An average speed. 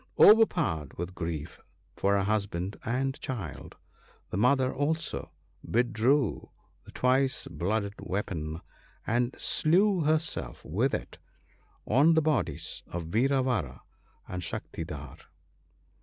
No: slow, 110 wpm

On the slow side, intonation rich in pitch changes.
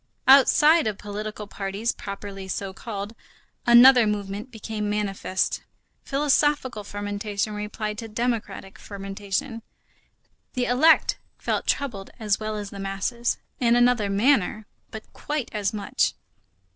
No: slow, 120 wpm; average, 3.2 semitones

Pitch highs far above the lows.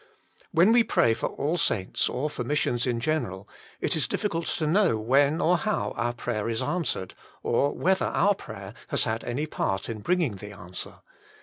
Yes: wide, 7.2 semitones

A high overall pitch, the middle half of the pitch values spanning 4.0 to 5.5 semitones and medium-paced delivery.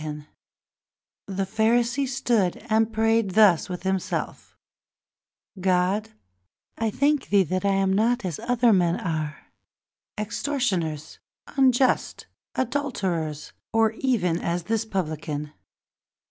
No: high, 205 Hz; average, 4.7 semitones; slow, 105 wpm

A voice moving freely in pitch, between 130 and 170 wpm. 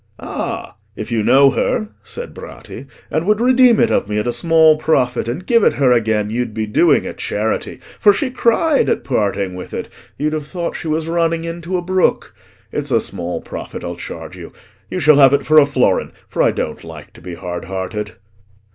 No: wide, 8.0 semitones; fast, 205 wpm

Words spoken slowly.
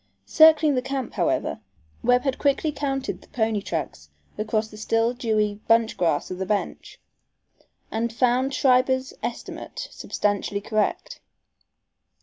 Yes: slow, 125 wpm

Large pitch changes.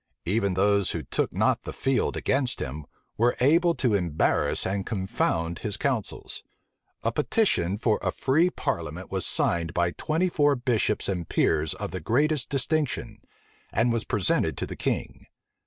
Yes: wide, 7.0 semitones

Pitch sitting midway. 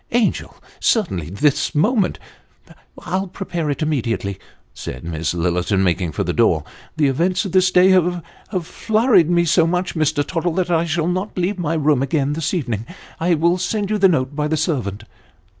Yes: medium, 165 Hz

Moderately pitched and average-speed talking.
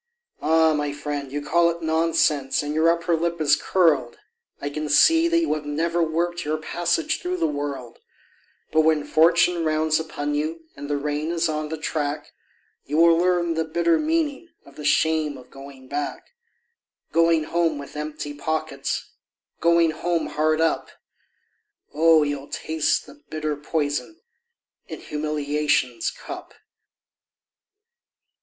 Yes: medium, 155 Hz; average, 145 wpm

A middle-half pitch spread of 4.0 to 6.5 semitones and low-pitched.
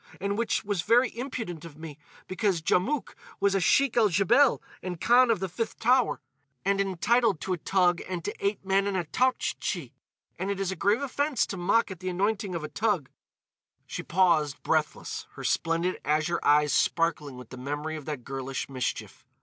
No: average, 5.1 semitones; high, 190 Hz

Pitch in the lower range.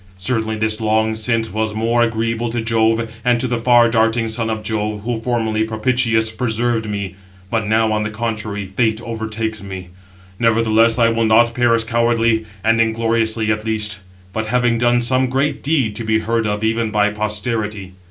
Yes: low, 110 Hz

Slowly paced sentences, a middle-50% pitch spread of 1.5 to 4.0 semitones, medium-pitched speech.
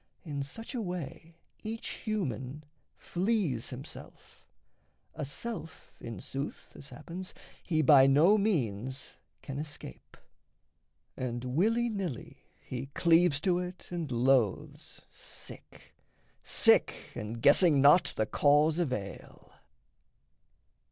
No: slow, 110 wpm; wide, 5.5 semitones; medium, 150 Hz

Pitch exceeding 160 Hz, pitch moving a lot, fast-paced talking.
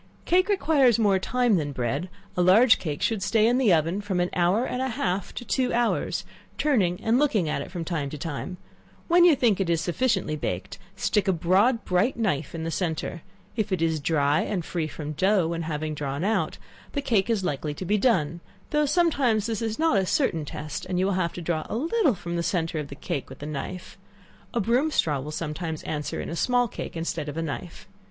Yes: medium, 185 Hz; wide, 6.3 semitones; fast, 220 wpm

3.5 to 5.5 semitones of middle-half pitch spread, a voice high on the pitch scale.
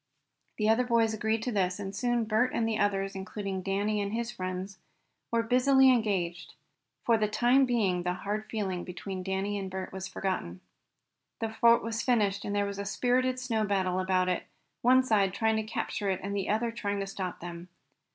No: average, 3.1 semitones; high, 205 Hz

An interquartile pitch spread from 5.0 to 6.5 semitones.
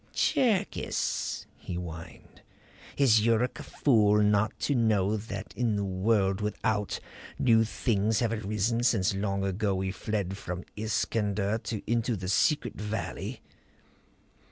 No: average, 2.7 semitones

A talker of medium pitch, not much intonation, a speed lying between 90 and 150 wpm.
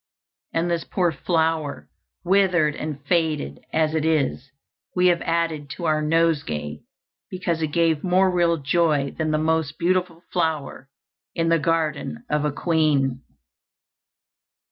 Yes: medium, 160 Hz; narrow, 2.2 semitones; slow, 135 wpm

